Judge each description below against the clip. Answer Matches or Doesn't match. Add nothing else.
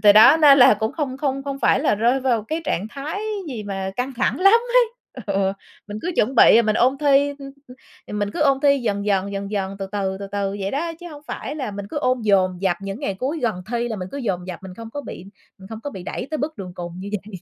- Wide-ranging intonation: Matches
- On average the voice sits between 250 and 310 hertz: Doesn't match